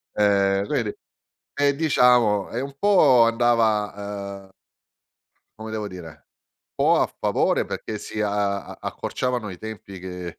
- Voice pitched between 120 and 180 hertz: No, low, 105 Hz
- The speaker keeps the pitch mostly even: No, average, 3.4 semitones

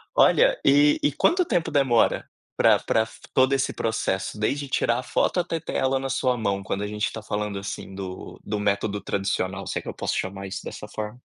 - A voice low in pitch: Yes, low, 110 Hz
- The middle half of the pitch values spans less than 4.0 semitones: No, average, 5.2 semitones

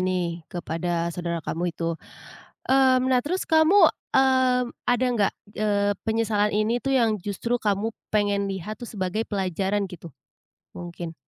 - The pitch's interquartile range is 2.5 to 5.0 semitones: No, wide, 5.4 semitones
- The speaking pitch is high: Yes, high, 205 Hz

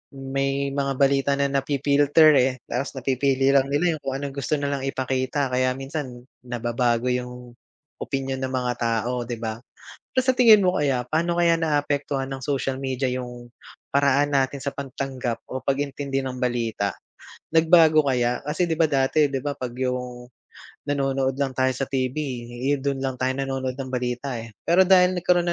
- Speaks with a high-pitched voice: No, low, 135 Hz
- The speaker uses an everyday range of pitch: No, narrow, 2.0 semitones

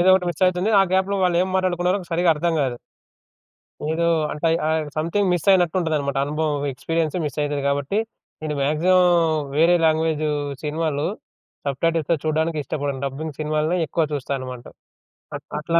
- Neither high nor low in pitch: Yes, medium, 160 Hz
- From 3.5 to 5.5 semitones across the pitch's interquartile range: No, average, 3.0 semitones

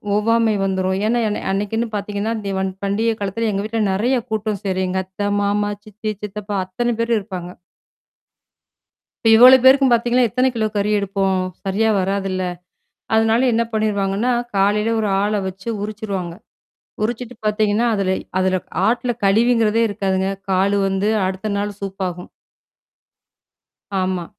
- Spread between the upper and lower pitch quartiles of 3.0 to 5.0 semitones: No, narrow, 2.6 semitones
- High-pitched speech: Yes, high, 205 Hz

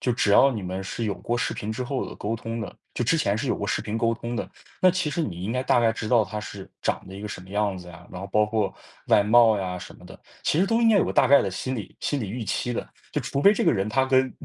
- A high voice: No, low, 115 Hz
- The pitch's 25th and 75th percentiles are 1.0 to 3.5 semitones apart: No, average, 4.3 semitones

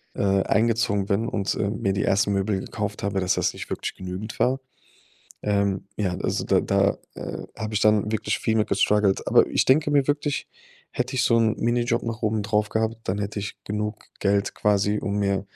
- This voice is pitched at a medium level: No, low, 105 Hz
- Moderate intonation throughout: No, narrow, 2.0 semitones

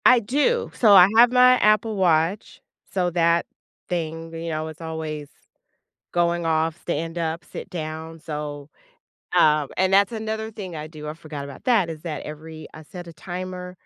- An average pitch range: Yes, average, 3.2 semitones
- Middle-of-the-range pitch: Yes, medium, 165 Hz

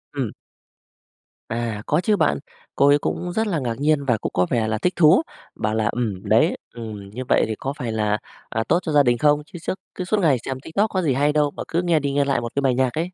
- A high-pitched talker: No, medium, 140 Hz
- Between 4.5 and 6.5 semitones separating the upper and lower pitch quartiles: Yes, wide, 5.6 semitones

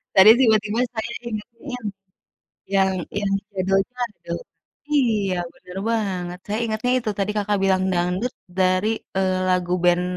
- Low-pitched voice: No, high, 205 Hz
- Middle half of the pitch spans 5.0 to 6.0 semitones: No, average, 3.0 semitones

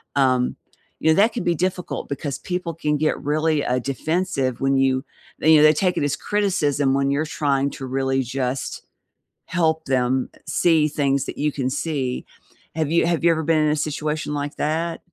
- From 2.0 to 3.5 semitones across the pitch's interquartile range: Yes, average, 2.9 semitones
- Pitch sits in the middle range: Yes, medium, 150 Hz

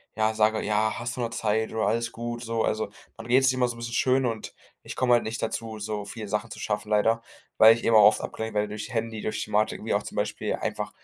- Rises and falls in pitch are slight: Yes, narrow, 1.5 semitones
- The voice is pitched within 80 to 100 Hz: No, low, 110 Hz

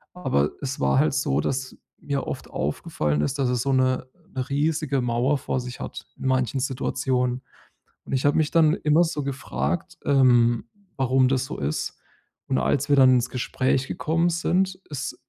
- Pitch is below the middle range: Yes, low, 130 Hz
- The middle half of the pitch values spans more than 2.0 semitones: Yes, narrow, 2.6 semitones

